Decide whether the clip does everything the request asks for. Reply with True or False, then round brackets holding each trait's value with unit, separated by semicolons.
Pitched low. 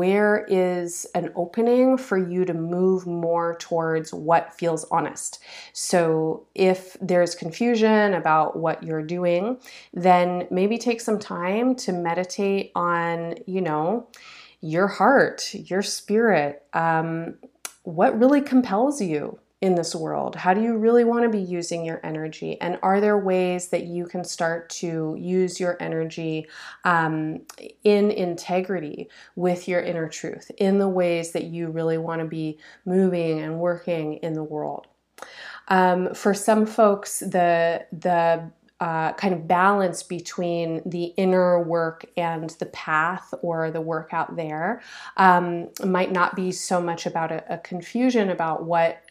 False (175 Hz)